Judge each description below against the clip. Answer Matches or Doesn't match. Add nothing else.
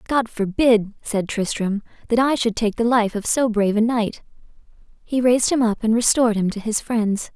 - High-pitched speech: Matches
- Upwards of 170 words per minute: Matches